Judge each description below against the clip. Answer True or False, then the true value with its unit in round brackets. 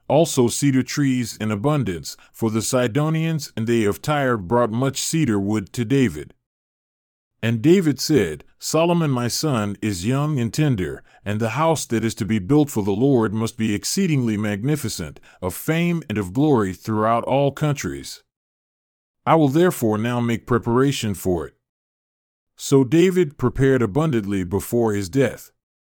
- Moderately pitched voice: False (120 Hz)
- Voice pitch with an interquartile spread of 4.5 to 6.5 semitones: True (5.4 semitones)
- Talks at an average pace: True (150 wpm)